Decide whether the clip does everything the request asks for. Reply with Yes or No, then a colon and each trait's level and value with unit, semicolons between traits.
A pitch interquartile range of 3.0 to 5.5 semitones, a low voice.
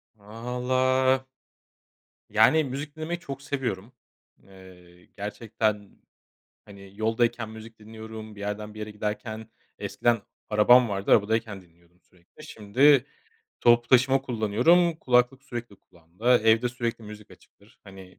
Yes: average, 3.4 semitones; low, 110 Hz